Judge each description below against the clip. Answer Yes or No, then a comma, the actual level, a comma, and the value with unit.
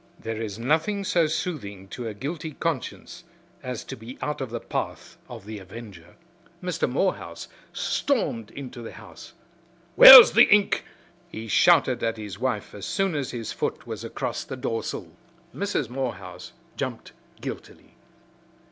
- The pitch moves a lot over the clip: Yes, wide, 6.4 semitones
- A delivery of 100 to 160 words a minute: Yes, average, 145 wpm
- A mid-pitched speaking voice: No, low, 125 Hz